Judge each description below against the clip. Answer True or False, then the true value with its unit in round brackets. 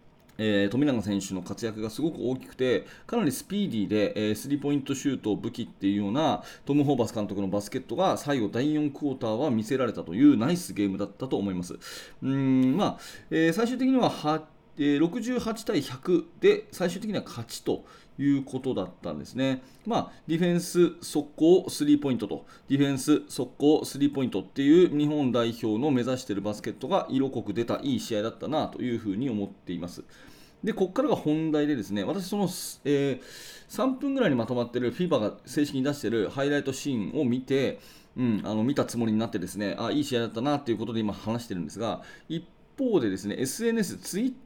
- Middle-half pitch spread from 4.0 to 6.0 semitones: False (7.0 semitones)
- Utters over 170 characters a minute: True (420 characters per minute)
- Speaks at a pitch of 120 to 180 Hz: True (135 Hz)